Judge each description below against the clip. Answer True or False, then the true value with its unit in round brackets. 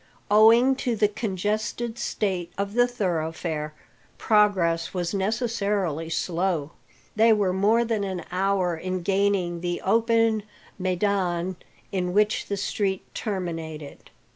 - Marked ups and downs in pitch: False (3.4 semitones)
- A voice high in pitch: True (195 Hz)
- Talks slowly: True (115 wpm)